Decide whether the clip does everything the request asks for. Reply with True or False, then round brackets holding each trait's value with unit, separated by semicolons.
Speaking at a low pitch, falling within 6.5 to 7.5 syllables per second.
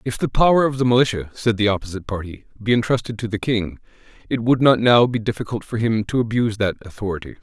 True (110 Hz; 6.6 syllables/s)